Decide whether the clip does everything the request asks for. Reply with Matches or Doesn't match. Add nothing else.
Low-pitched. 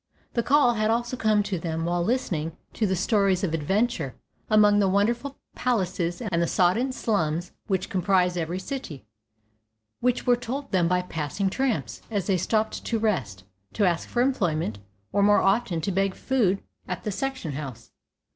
Doesn't match